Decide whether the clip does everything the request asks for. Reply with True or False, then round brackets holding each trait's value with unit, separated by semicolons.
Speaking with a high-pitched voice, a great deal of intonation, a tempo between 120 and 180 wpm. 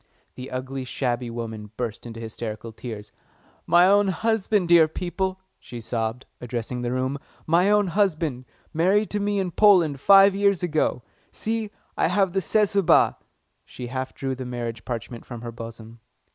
False (135 Hz; 8.1 semitones; 160 wpm)